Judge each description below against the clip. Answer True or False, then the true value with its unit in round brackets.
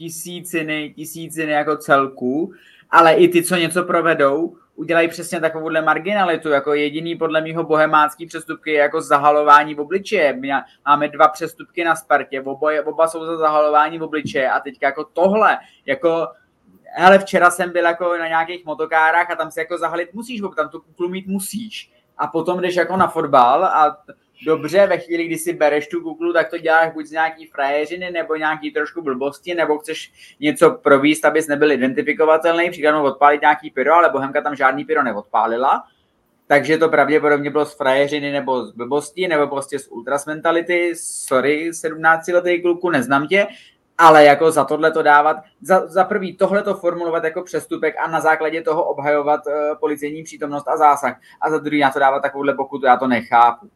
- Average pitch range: False (2.3 semitones)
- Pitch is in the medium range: True (155 Hz)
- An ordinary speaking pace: False (175 wpm)